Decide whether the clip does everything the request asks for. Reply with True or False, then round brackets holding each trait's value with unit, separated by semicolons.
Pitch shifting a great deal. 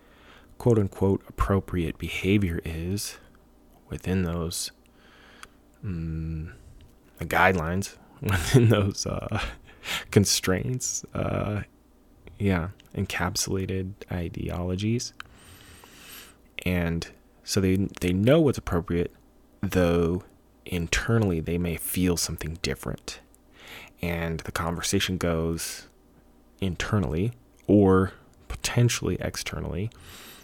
False (2.9 semitones)